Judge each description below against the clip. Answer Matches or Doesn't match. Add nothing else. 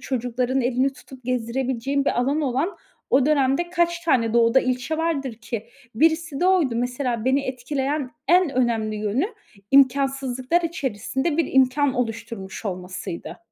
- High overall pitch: Matches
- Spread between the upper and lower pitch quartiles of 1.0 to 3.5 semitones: Matches